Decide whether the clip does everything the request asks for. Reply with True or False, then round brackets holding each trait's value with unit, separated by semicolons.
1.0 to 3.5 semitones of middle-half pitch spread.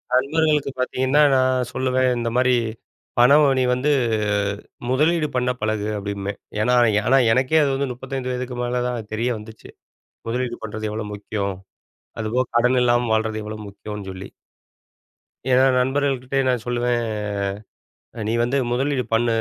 True (2.8 semitones)